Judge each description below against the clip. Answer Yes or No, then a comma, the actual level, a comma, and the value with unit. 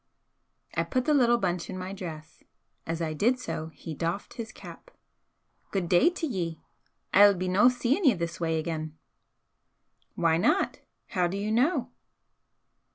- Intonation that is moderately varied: No, wide, 6.3 semitones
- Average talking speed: Yes, average, 155 wpm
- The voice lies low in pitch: No, medium, 185 Hz